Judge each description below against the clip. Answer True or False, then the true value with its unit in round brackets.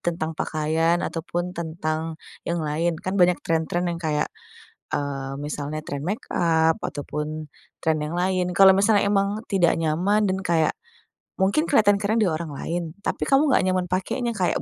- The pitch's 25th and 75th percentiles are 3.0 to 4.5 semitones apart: True (3.4 semitones)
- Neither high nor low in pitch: True (170 Hz)